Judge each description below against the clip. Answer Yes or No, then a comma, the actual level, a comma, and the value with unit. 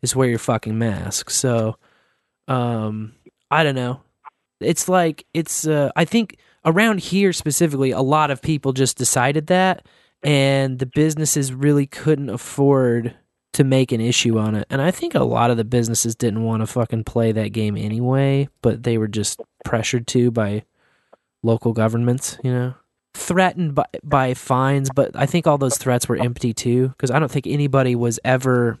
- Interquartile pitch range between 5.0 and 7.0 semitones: No, average, 3.7 semitones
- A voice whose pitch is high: No, low, 130 Hz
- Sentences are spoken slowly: No, average, 175 wpm